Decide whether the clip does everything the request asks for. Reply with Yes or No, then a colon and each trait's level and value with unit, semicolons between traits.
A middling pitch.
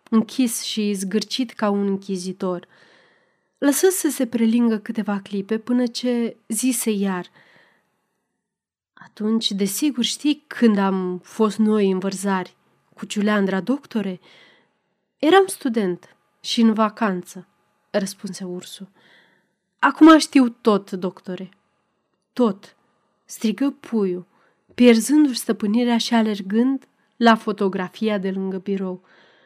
No: high, 215 Hz